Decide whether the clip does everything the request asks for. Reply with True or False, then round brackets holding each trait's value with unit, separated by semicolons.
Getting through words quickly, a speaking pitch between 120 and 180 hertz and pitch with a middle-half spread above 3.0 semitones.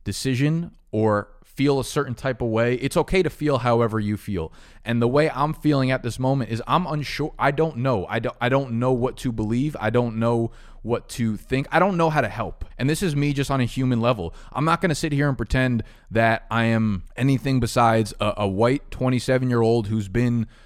True (230 wpm; 125 Hz; 3.4 semitones)